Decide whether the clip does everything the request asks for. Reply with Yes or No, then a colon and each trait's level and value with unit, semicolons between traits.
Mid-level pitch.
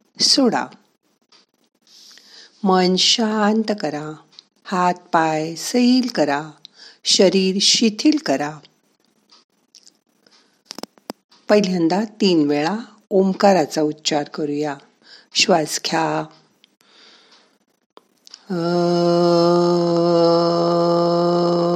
Yes: medium, 175 Hz